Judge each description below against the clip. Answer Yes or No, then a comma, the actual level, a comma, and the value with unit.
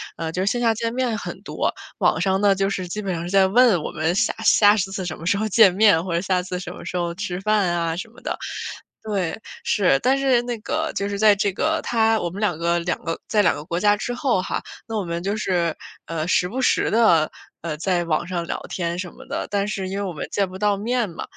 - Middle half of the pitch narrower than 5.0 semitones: Yes, average, 3.7 semitones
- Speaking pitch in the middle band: No, high, 195 Hz